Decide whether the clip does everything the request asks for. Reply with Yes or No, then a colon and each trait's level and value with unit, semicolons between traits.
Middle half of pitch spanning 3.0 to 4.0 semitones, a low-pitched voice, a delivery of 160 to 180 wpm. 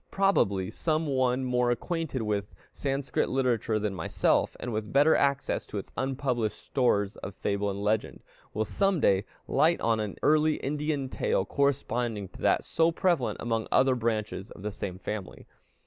No: average, 5.1 semitones; low, 125 Hz; average, 165 wpm